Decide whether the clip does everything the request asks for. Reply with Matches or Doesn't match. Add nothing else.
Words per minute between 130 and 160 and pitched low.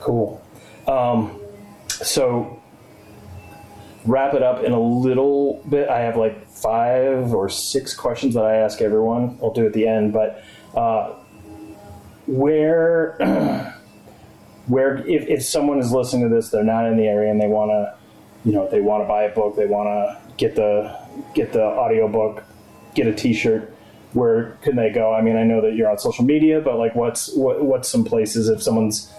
Doesn't match